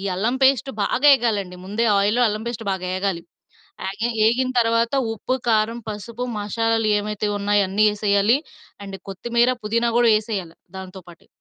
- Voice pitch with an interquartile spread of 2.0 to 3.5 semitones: Yes, narrow, 2.6 semitones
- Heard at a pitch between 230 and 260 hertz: No, high, 215 Hz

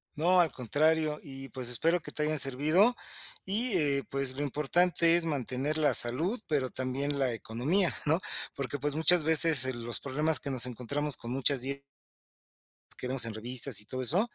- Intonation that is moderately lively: Yes, average, 3.8 semitones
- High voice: No, medium, 140 Hz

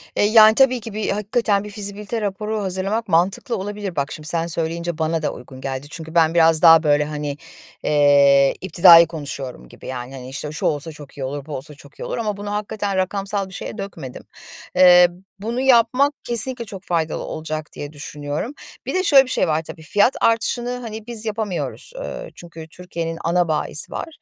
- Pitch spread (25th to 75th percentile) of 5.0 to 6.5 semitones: Yes, wide, 5.6 semitones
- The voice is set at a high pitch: No, medium, 175 Hz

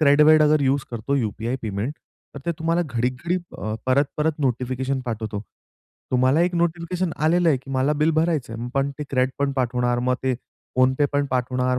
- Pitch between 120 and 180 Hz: Yes, low, 135 Hz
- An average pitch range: Yes, average, 3.4 semitones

